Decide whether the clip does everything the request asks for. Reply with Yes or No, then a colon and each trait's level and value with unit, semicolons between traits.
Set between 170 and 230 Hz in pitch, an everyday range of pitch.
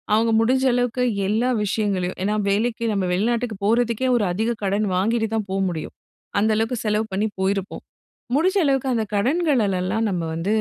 Yes: high, 220 Hz; average, 3.3 semitones